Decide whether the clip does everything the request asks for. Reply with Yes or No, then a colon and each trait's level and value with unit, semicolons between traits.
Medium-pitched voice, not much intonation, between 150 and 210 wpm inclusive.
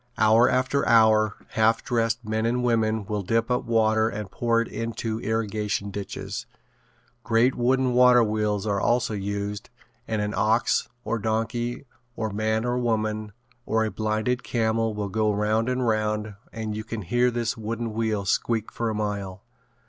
No: low, 110 Hz; narrow, 1.5 semitones; average, 160 wpm